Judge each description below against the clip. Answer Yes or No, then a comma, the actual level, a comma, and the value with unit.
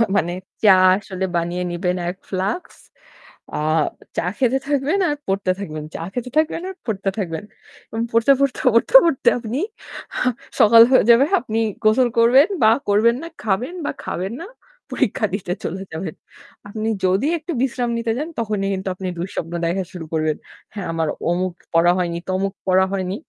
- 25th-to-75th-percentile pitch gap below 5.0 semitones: Yes, average, 4.5 semitones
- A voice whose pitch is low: No, high, 200 Hz